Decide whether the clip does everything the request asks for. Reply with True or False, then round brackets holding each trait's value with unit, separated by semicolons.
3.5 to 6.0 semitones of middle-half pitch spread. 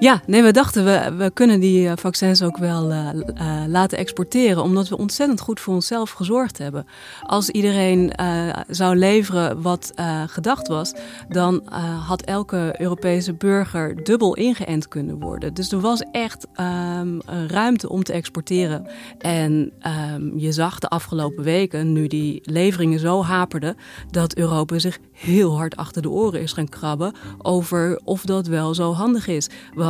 False (3.1 semitones)